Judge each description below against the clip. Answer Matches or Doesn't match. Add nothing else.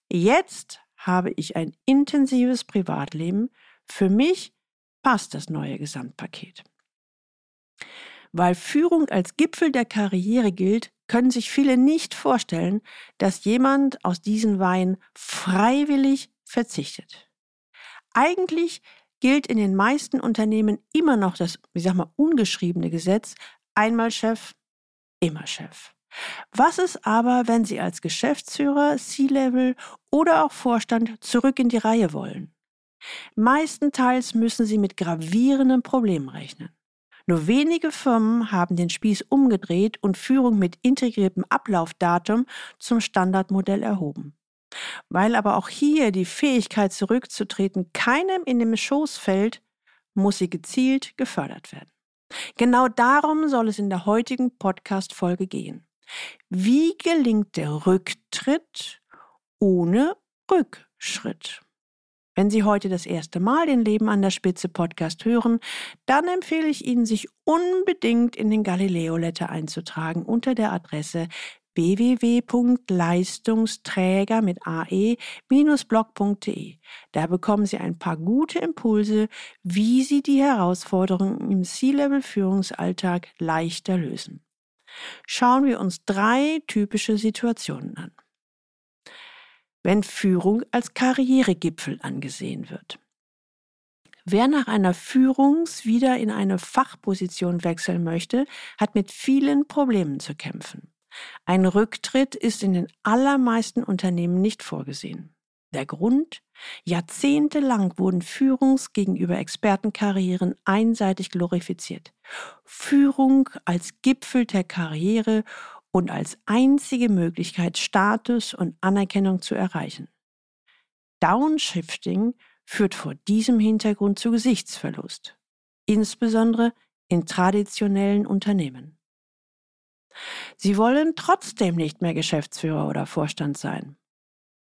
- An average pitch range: Doesn't match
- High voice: Matches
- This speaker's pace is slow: Matches